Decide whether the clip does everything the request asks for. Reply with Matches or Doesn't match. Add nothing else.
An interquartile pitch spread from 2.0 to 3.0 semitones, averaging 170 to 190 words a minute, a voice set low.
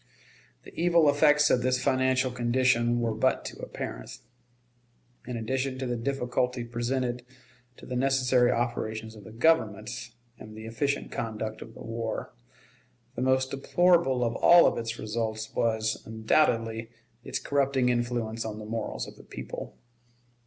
Doesn't match